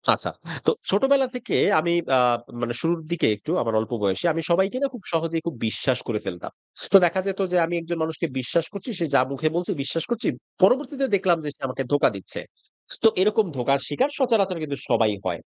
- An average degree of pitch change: No, wide, 6.6 semitones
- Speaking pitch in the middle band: Yes, medium, 165 Hz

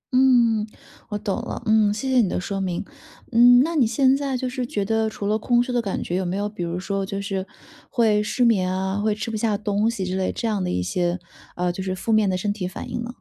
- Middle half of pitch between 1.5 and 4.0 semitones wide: Yes, average, 3.6 semitones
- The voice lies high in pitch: Yes, high, 210 Hz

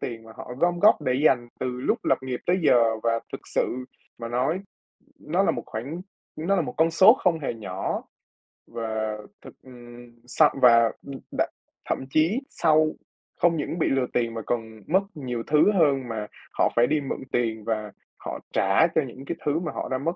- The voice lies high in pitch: No, low, 130 Hz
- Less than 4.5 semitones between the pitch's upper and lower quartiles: No, average, 5.3 semitones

